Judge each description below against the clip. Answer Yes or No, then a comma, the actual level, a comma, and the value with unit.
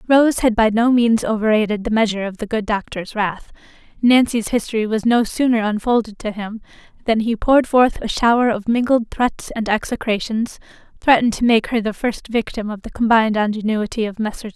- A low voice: No, high, 225 Hz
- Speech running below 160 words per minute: No, average, 185 wpm